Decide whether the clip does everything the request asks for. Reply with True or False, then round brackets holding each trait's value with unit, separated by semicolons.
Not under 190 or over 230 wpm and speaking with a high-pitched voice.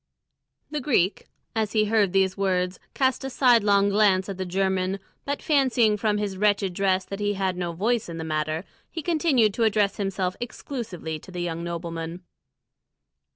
False (170 wpm; 195 Hz)